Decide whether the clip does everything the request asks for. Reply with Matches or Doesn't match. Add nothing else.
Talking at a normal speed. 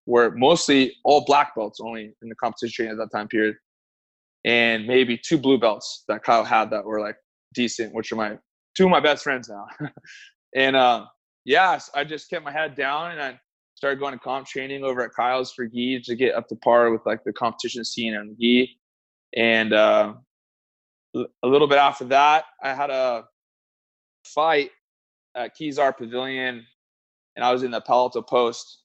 Matches